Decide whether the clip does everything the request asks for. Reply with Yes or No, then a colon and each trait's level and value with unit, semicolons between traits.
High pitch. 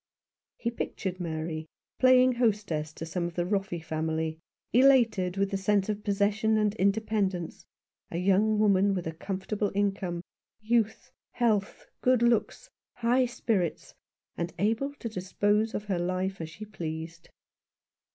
Yes: high, 200 Hz